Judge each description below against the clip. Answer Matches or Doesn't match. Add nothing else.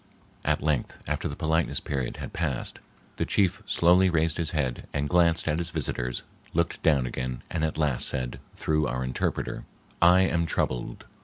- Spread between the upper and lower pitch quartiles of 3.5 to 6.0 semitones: Matches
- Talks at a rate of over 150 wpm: Matches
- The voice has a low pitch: Matches